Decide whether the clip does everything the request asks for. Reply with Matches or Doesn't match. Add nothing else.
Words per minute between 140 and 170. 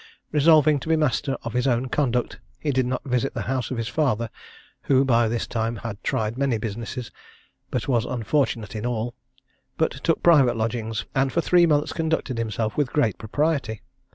Doesn't match